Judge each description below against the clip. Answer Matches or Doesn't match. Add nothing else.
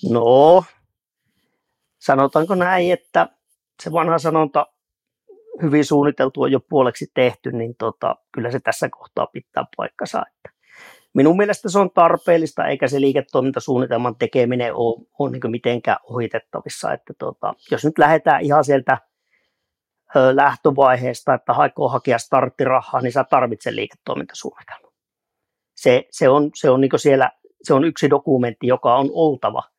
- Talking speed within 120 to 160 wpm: Matches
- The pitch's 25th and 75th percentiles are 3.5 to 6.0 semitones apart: Matches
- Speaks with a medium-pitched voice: Matches